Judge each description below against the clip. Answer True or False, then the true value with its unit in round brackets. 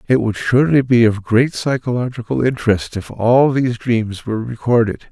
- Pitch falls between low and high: False (115 Hz)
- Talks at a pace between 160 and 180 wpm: True (165 wpm)